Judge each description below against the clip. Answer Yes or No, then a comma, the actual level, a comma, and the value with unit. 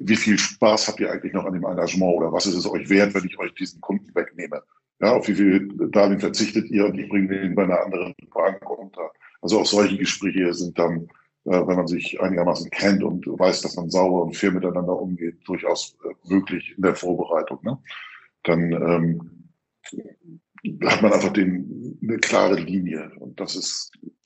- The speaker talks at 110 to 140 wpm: No, fast, 190 wpm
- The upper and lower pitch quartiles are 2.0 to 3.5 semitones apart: Yes, narrow, 2.4 semitones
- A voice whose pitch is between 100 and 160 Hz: No, very low, 90 Hz